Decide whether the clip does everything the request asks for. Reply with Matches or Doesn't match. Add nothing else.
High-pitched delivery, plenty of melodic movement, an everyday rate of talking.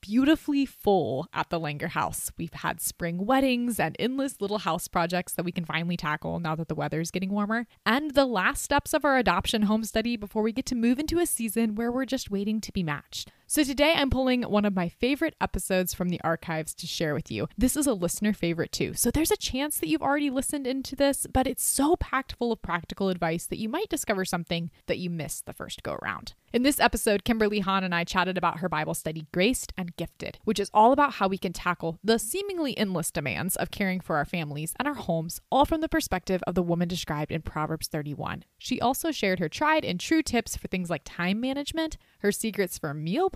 Doesn't match